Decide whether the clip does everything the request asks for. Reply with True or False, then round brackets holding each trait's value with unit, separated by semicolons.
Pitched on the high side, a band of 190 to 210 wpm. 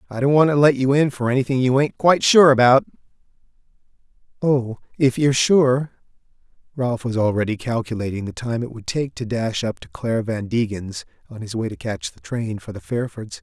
False (120 Hz; 195 wpm)